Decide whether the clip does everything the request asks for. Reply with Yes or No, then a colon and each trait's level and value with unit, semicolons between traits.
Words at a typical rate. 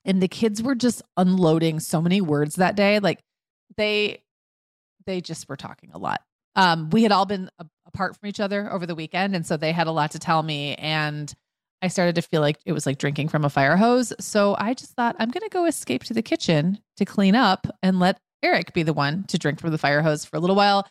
No: fast, 245 wpm